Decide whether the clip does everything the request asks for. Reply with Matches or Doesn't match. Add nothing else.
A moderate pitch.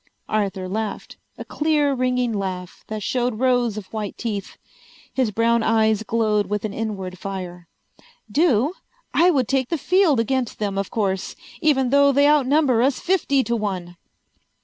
Doesn't match